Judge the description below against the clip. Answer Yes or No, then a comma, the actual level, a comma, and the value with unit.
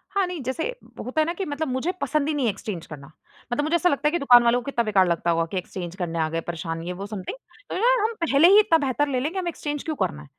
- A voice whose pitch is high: Yes, very high, 265 Hz